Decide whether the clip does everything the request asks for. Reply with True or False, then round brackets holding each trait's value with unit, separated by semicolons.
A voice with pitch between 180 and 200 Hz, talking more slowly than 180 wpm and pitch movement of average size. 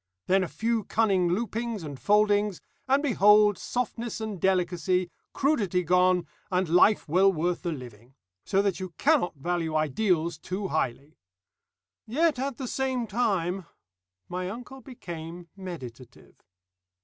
True (185 Hz; 135 wpm; 4.6 semitones)